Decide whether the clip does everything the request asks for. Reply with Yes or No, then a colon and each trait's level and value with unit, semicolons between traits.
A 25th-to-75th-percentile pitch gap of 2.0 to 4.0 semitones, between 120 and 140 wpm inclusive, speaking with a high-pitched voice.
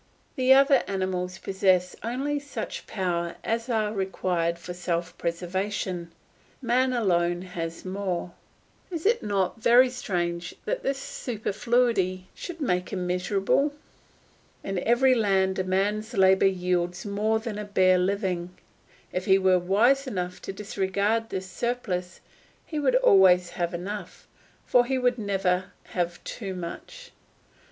No: average, 4.5 semitones; slow, 135 wpm; high, 195 Hz